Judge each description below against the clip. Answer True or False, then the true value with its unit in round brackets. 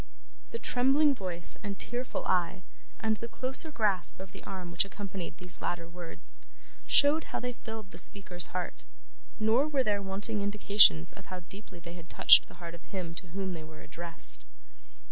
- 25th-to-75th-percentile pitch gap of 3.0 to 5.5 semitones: True (4.1 semitones)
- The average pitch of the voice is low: False (195 Hz)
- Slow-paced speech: False (180 wpm)